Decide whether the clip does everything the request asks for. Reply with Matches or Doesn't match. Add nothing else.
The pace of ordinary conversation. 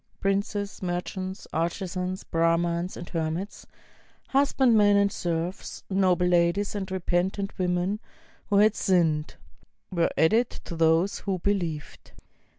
Doesn't match